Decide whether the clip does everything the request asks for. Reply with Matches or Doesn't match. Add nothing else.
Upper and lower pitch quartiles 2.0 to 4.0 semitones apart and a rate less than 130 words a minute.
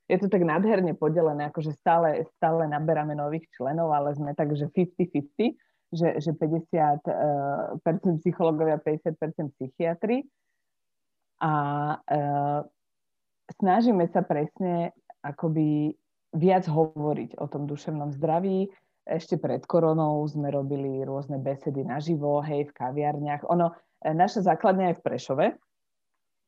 Matches